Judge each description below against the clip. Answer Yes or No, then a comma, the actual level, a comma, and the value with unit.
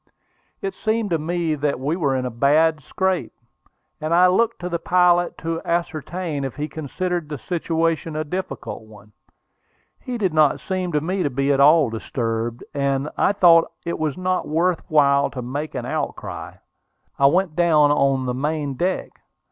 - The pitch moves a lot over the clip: No, average, 4.0 semitones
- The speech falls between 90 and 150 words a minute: No, average, 175 wpm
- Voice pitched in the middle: Yes, medium, 155 Hz